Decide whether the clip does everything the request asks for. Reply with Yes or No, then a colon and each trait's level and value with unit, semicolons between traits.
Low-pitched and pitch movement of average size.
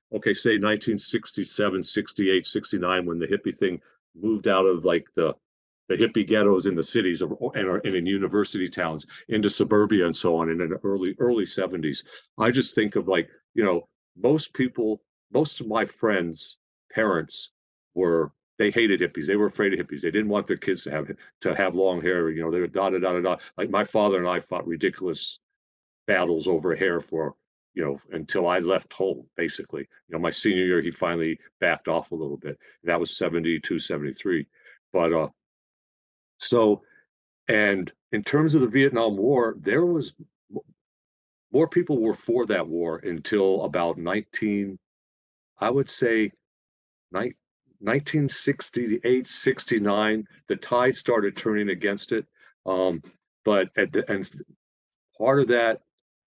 Yes: low, 100 Hz; average, 4.2 semitones